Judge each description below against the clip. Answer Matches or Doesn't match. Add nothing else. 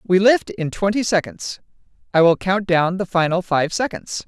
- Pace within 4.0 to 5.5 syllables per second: Matches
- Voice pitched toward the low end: Doesn't match